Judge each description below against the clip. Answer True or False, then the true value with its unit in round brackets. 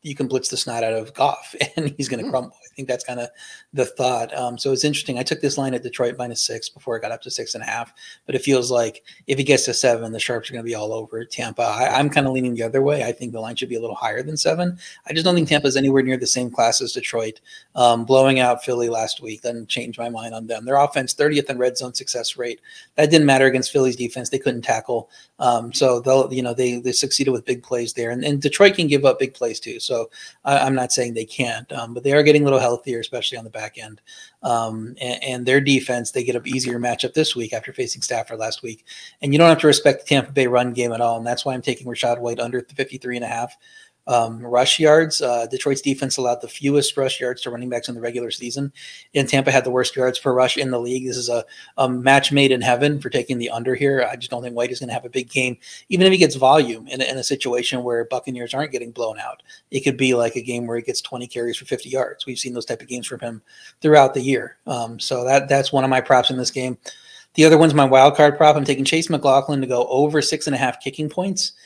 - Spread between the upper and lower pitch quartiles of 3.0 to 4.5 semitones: False (2.6 semitones)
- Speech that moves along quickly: True (275 wpm)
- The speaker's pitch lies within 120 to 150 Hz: True (130 Hz)